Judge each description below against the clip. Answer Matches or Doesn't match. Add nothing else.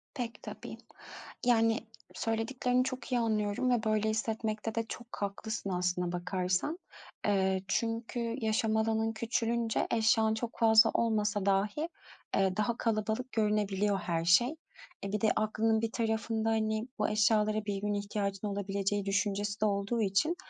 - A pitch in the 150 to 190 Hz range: Doesn't match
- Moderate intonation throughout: Doesn't match